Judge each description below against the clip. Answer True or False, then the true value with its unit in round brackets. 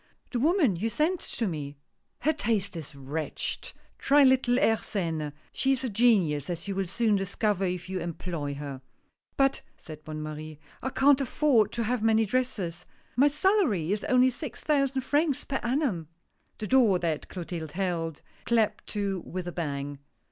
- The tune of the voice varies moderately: False (7.6 semitones)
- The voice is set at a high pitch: True (205 Hz)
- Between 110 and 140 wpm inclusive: False (180 wpm)